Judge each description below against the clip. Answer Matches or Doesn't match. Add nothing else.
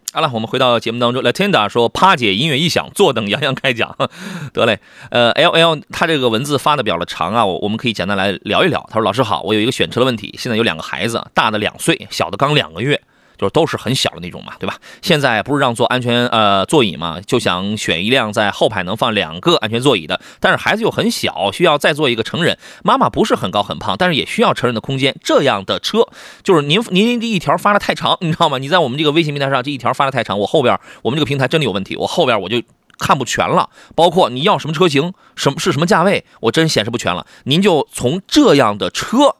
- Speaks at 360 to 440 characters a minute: Matches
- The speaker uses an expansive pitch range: Matches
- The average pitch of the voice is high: Doesn't match